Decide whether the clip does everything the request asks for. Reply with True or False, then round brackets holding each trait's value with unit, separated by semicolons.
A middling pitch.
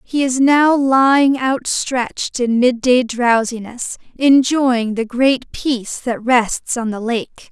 False (250 Hz)